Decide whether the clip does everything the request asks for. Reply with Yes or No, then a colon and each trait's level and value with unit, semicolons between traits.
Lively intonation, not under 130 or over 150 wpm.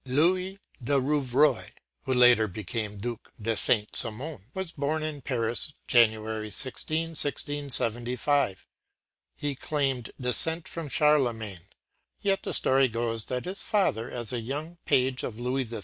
No: average, 4.6 semitones; average, 145 wpm